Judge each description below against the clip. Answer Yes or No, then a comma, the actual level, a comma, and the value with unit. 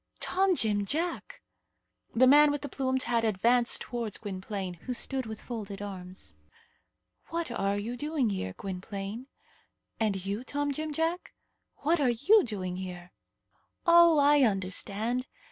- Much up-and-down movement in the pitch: Yes, wide, 6.4 semitones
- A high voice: Yes, high, 235 Hz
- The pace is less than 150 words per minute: Yes, average, 140 wpm